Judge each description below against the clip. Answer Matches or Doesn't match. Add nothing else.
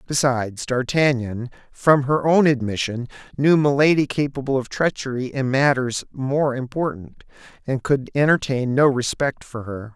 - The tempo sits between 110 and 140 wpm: Matches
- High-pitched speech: Doesn't match